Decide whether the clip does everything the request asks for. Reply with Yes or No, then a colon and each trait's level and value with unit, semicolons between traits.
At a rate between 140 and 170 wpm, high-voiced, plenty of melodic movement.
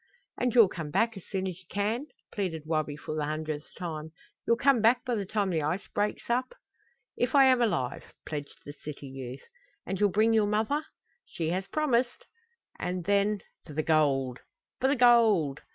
No: average, 185 wpm; high, 195 Hz; wide, 7.0 semitones